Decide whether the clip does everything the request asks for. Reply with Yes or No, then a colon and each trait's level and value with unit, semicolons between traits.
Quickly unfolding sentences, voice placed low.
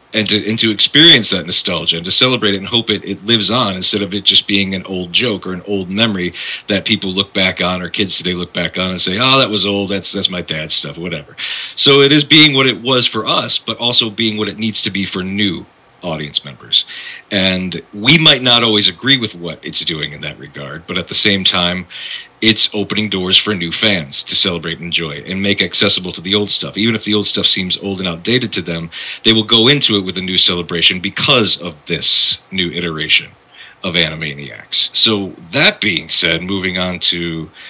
Yes: fast, 230 wpm; low, 100 Hz